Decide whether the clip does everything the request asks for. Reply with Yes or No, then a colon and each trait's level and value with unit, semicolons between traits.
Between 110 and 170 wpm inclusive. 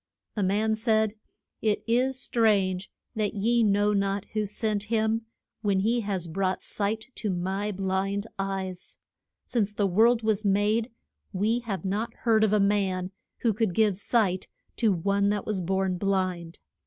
Yes: average, 155 wpm